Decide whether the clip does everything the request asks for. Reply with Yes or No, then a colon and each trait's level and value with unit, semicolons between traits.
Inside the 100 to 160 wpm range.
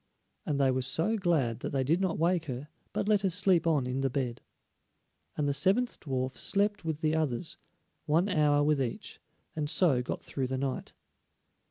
No: average, 190 wpm